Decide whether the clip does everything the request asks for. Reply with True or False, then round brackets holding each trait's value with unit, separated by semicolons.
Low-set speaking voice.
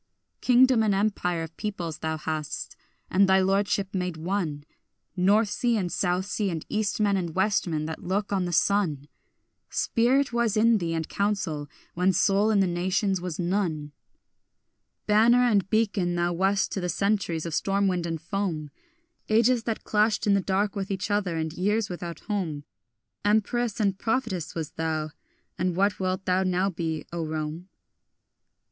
False (190 Hz)